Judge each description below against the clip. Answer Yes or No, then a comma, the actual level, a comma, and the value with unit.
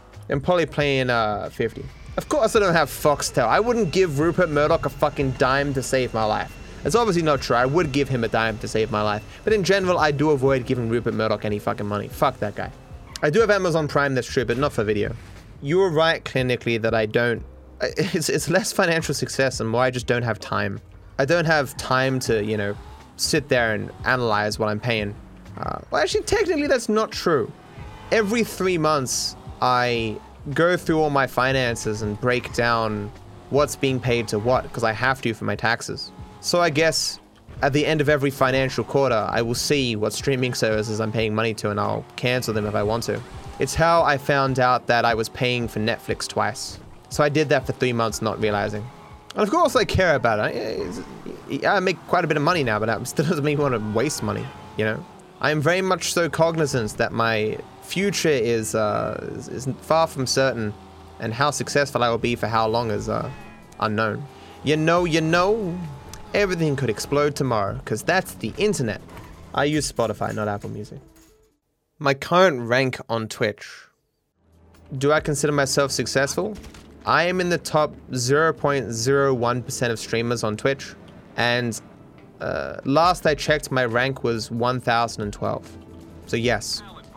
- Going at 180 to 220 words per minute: Yes, average, 190 wpm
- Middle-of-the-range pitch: No, low, 125 Hz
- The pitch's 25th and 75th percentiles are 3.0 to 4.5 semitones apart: No, average, 5.2 semitones